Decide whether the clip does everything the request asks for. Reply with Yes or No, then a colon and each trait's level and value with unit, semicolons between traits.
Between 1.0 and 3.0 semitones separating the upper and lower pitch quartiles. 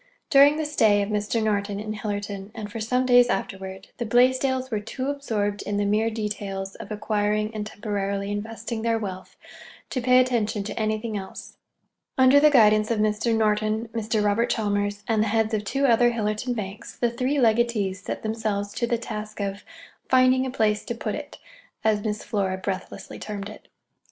Yes: narrow, 2.5 semitones